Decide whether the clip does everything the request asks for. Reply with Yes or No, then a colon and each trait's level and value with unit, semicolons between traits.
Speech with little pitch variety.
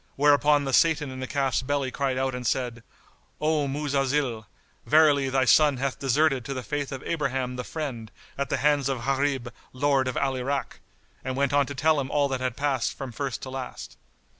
Yes: narrow, 1.8 semitones